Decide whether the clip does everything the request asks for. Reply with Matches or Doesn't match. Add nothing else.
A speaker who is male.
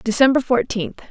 Doesn't match